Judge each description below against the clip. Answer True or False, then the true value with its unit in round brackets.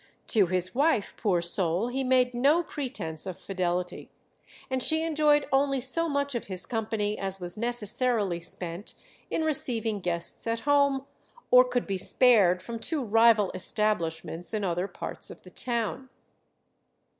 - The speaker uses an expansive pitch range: True (6.0 semitones)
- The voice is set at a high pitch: True (225 Hz)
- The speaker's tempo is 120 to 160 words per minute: True (150 wpm)